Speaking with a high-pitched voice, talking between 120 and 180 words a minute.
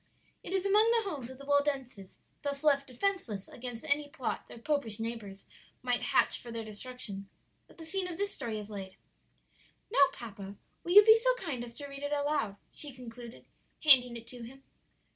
No: very high, 260 Hz; average, 190 wpm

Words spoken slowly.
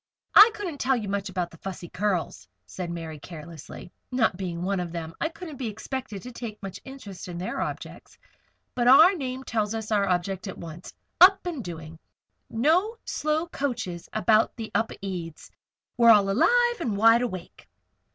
No: average, 170 wpm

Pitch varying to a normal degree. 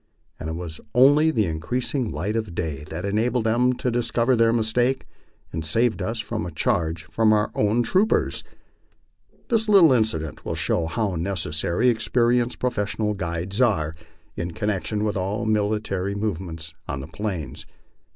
No: wide, 5.8 semitones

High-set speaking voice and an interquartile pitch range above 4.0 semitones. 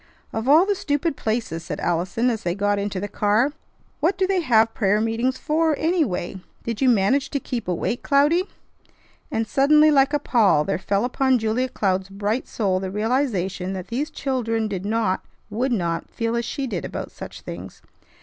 Yes: high, 225 Hz; wide, 5.5 semitones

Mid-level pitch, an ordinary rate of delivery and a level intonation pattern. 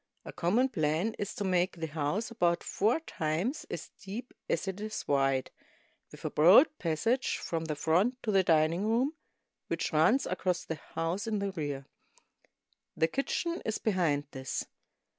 No: medium, 180 Hz; average, 160 wpm; wide, 5.6 semitones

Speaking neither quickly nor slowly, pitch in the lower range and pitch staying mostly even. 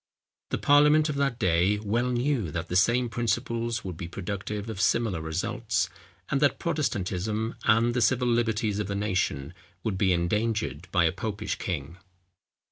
No: average, 160 wpm; low, 105 Hz; average, 4.4 semitones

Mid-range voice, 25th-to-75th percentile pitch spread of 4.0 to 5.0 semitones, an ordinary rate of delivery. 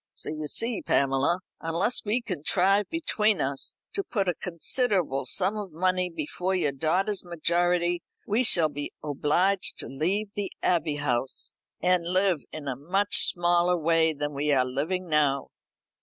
Yes: medium, 175 Hz; average, 4.4 semitones; average, 155 wpm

